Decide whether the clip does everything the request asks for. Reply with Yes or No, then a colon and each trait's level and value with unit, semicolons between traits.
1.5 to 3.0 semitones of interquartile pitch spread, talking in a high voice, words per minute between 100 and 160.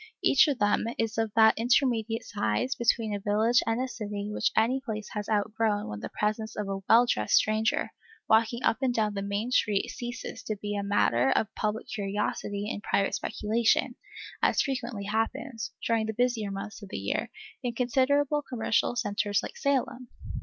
No: average, 2.7 semitones; high, 220 Hz; average, 180 wpm